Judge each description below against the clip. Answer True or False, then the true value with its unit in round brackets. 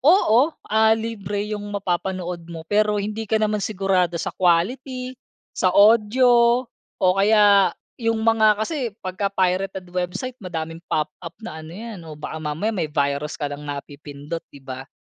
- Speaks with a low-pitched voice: False (195 Hz)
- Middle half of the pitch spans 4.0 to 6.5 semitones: True (4.7 semitones)